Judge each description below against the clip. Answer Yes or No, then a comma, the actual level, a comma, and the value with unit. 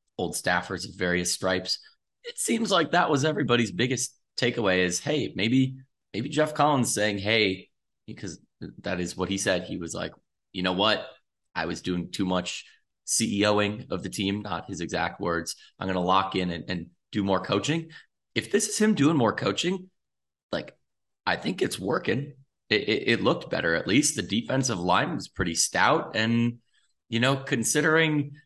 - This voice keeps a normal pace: Yes, average, 180 wpm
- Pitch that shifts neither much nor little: No, wide, 7.4 semitones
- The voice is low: Yes, low, 105 Hz